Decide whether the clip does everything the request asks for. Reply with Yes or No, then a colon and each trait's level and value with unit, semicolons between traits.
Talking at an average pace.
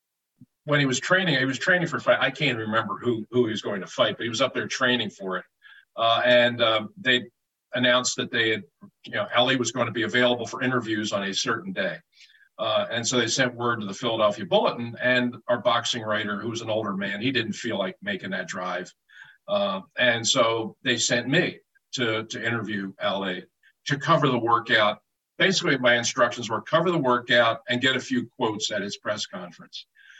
No: fast, 210 wpm